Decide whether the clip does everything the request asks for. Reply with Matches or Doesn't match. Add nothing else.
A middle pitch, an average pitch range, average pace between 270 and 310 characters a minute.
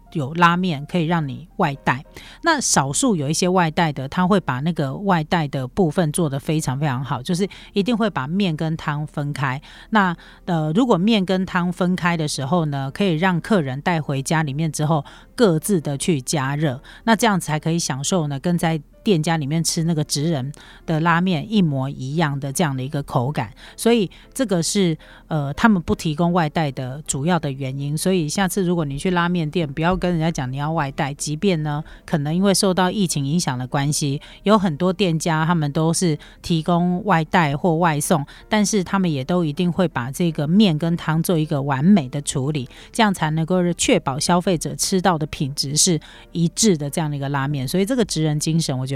Matches